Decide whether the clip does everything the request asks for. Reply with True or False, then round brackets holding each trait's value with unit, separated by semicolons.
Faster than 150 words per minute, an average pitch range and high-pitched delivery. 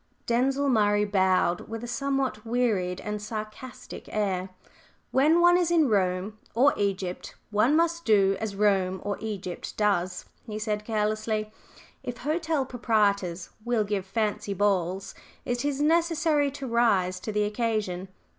False (140 wpm; 4.4 semitones; 215 Hz)